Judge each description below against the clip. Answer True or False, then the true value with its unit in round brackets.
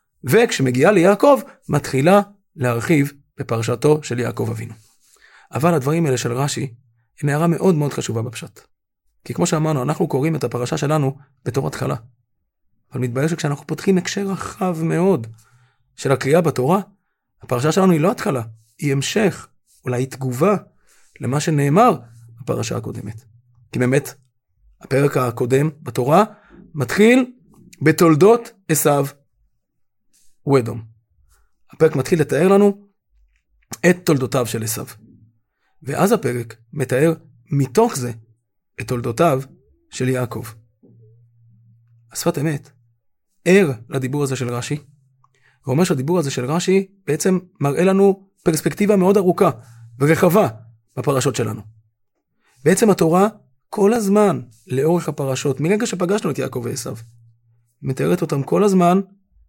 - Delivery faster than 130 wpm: False (115 wpm)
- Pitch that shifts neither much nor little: False (6.5 semitones)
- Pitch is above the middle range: False (140 Hz)